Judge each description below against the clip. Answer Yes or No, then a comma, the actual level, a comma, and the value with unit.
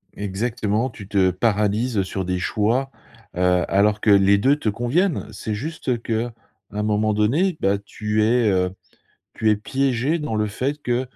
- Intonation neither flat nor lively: Yes, average, 3.6 semitones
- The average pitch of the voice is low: Yes, low, 110 Hz